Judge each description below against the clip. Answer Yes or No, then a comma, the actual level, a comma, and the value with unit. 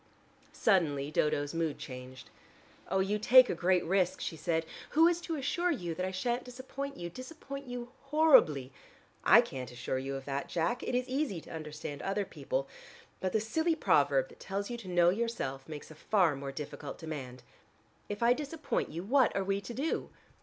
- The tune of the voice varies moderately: No, wide, 9.0 semitones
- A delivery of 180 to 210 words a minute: Yes, average, 190 wpm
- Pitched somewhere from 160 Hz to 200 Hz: Yes, high, 190 Hz